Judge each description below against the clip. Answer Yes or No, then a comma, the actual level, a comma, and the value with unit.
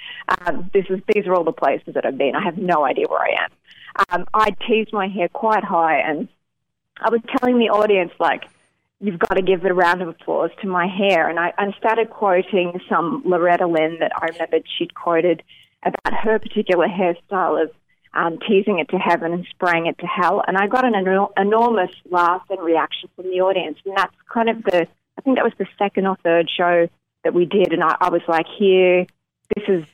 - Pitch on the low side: No, medium, 185 Hz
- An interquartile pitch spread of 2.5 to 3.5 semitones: Yes, average, 3.2 semitones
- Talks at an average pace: No, fast, 215 wpm